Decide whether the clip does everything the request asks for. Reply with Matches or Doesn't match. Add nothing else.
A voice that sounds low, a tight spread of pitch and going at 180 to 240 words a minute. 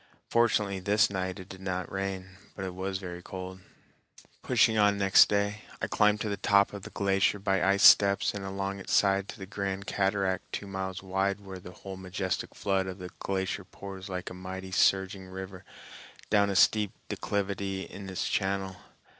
Matches